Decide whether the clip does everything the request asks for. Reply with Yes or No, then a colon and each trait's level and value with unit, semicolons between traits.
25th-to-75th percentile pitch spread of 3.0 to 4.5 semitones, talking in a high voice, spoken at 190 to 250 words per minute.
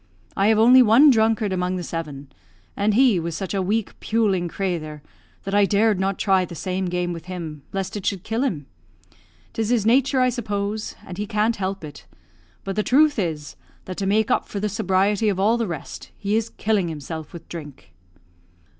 Yes: average, 3.7 semitones; high, 195 Hz; average, 200 wpm